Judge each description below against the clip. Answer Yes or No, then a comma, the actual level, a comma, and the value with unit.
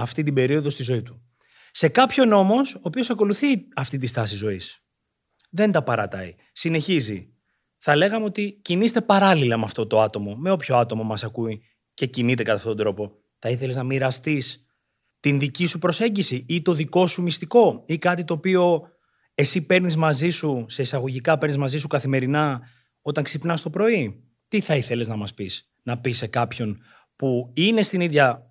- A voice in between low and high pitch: Yes, medium, 145 Hz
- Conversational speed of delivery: No, fast, 180 wpm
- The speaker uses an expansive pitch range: Yes, wide, 6.8 semitones